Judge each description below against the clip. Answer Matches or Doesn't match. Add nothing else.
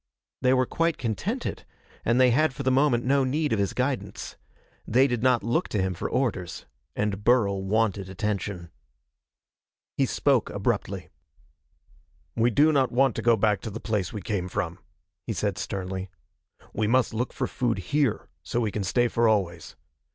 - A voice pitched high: Doesn't match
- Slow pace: Doesn't match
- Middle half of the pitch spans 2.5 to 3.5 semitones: Doesn't match